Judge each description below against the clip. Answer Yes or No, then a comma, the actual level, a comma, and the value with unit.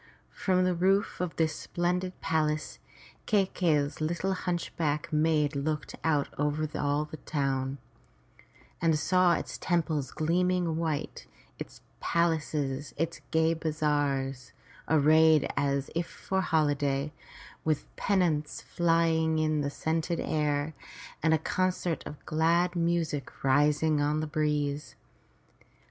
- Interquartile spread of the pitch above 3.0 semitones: No, narrow, 2.4 semitones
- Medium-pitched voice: Yes, medium, 155 Hz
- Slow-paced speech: Yes, slow, 115 wpm